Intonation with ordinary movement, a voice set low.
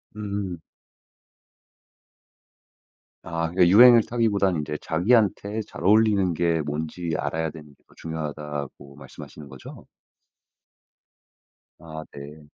Yes: average, 4.9 semitones; very low, 85 Hz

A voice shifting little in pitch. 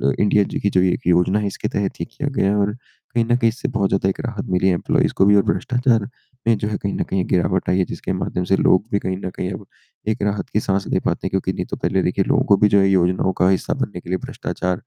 Yes: narrow, 2.2 semitones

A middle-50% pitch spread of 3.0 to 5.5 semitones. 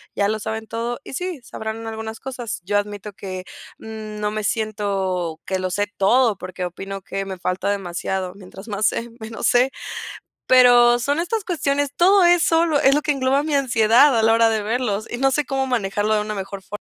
Yes: average, 4.6 semitones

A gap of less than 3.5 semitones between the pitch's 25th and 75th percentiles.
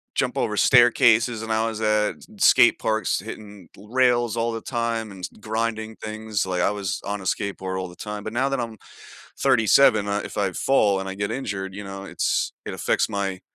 Yes: narrow, 2.5 semitones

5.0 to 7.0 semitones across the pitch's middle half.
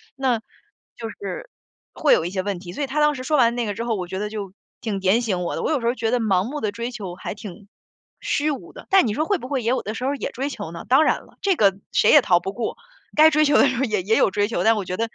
Yes: wide, 5.5 semitones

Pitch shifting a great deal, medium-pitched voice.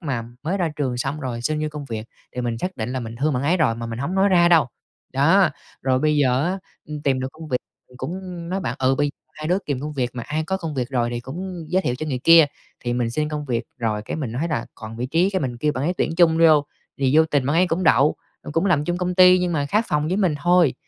No: average, 5.0 semitones; medium, 150 Hz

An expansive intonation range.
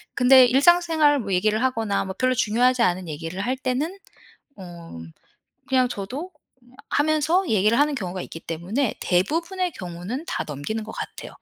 Yes: wide, 7.4 semitones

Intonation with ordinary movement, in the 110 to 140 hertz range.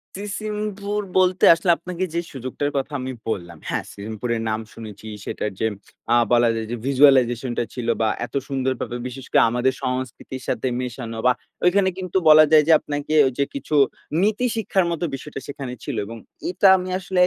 No: wide, 7.0 semitones; low, 135 Hz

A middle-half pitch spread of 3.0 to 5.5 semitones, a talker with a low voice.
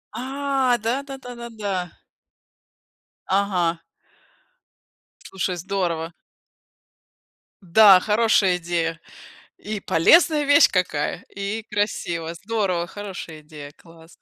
No: average, 5.0 semitones; high, 195 Hz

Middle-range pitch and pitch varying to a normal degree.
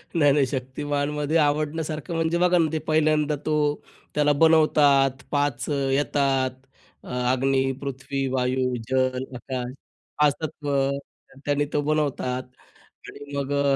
No: medium, 145 Hz; narrow, 2.2 semitones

